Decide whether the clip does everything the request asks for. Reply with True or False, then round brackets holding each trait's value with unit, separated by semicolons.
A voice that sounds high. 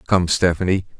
False (90 Hz)